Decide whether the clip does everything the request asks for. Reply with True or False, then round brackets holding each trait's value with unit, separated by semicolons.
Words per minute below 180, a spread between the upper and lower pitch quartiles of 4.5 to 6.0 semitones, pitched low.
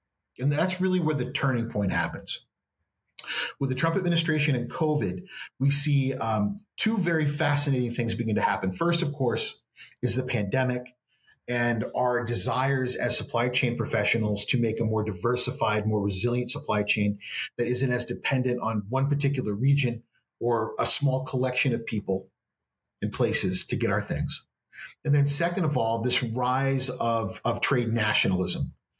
False (160 wpm; 3.3 semitones; 125 Hz)